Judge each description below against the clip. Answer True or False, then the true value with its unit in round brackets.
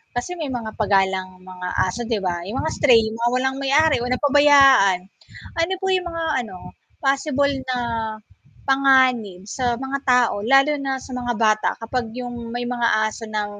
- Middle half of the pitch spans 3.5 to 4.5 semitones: True (4.0 semitones)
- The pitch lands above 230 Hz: True (250 Hz)